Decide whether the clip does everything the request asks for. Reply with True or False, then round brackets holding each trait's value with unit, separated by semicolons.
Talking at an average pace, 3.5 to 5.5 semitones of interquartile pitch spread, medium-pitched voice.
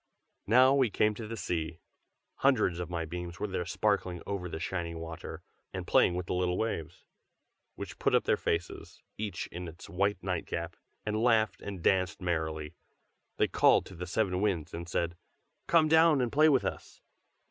False (180 wpm; 4.2 semitones; 90 Hz)